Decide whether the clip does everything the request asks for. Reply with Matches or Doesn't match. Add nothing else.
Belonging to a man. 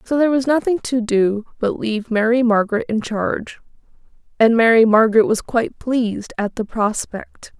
Doesn't match